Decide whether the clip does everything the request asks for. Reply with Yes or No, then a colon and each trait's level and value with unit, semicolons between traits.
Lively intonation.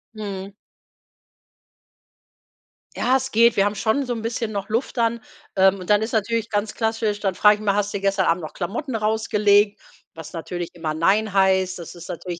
No: average, 2.7 semitones